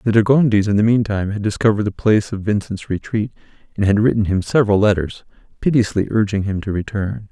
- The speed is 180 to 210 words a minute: Yes, average, 195 wpm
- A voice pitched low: Yes, low, 105 Hz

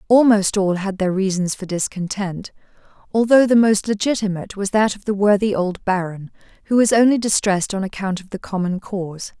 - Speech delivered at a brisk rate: No, average, 180 wpm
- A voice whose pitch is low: No, high, 200 Hz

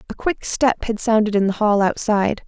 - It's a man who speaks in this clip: No, female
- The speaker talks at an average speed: No, fast, 220 wpm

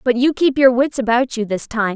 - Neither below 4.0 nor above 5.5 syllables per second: Yes, 5.3 syllables/s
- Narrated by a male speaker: No, female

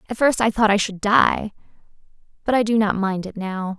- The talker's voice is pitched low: No, high, 210 Hz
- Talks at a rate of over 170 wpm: Yes, fast, 205 wpm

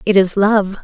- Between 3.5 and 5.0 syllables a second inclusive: Yes, 4.5 syllables/s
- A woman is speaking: Yes, female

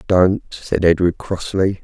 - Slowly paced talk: Yes, slow, 130 wpm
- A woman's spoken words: No, male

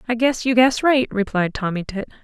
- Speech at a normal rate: No, fast, 215 wpm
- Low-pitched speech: No, high, 230 Hz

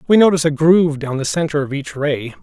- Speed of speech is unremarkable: No, fast, 250 wpm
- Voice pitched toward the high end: No, medium, 150 Hz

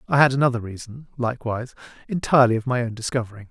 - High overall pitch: No, low, 120 Hz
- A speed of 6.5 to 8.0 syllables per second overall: Yes, 7.5 syllables/s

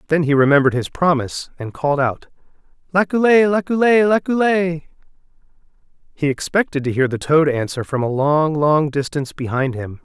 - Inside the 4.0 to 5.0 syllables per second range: No, 5.5 syllables/s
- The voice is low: No, medium, 155 Hz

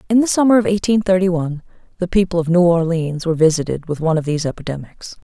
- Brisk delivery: Yes, fast, 215 wpm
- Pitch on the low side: No, medium, 175 Hz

